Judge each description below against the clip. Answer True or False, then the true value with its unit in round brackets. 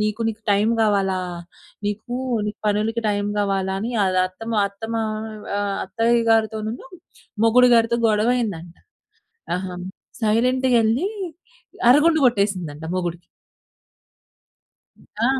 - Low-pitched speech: False (215 Hz)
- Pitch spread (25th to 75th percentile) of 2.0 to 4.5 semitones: True (2.6 semitones)